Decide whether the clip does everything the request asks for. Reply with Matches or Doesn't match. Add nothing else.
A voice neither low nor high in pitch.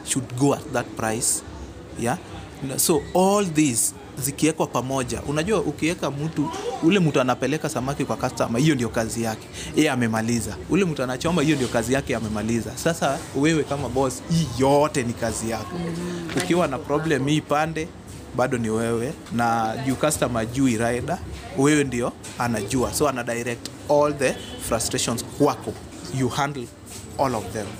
Doesn't match